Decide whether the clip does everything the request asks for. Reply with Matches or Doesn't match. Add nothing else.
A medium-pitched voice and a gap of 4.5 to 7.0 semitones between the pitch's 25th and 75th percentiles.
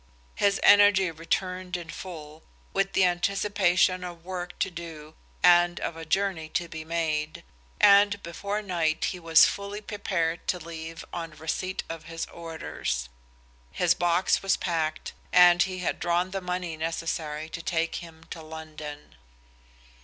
Doesn't match